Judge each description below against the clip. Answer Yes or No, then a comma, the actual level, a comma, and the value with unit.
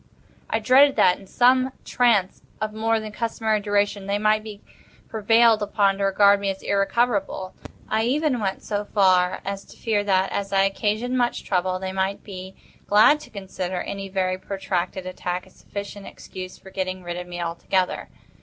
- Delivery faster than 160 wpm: Yes, average, 175 wpm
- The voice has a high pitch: Yes, high, 200 Hz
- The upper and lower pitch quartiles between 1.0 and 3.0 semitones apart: Yes, narrow, 2.5 semitones